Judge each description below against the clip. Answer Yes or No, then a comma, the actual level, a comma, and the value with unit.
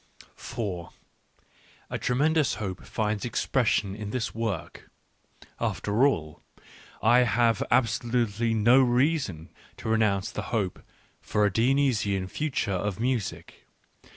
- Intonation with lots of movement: No, average, 3.6 semitones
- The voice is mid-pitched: No, low, 115 Hz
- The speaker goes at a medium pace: No, slow, 105 wpm